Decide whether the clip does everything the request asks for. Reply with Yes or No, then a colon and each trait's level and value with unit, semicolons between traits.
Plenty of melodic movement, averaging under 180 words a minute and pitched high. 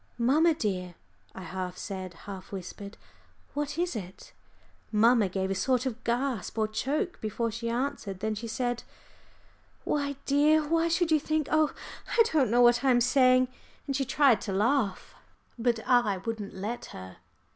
Yes: wide, 5.7 semitones; average, 165 wpm; high, 240 Hz